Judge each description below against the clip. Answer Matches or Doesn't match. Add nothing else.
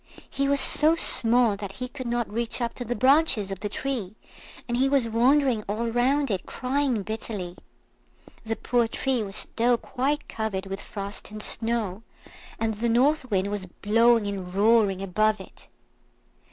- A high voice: Matches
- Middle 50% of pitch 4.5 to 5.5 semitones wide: Doesn't match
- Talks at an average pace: Matches